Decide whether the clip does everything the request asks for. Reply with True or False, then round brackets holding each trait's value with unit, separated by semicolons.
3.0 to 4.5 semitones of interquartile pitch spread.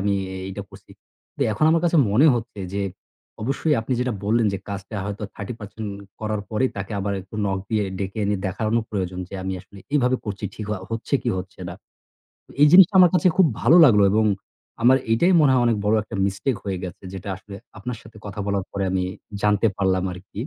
True (3.5 semitones)